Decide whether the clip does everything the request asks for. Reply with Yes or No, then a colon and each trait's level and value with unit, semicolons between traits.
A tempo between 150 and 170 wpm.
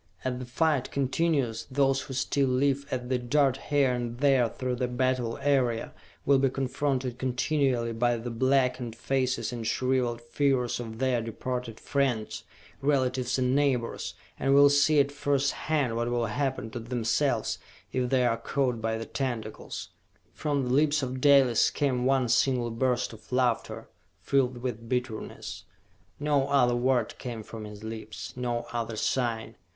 Yes: average, 155 wpm